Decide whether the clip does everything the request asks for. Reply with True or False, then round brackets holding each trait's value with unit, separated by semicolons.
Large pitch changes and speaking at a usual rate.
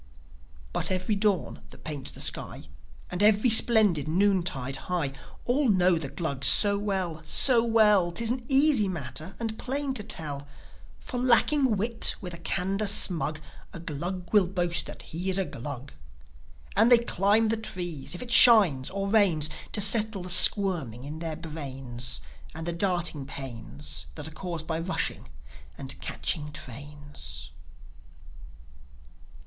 True (5.9 semitones; 150 wpm)